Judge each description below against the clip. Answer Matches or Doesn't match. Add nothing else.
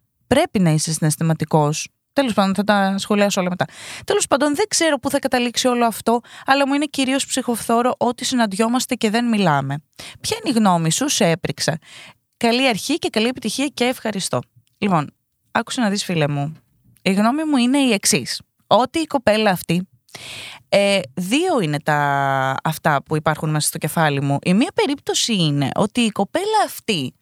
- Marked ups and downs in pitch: Matches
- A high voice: Matches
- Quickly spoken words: Matches